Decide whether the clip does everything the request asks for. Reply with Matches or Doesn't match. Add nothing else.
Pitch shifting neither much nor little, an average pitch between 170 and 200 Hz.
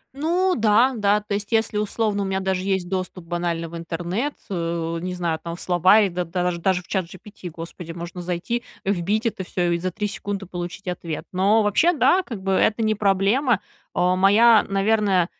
Matches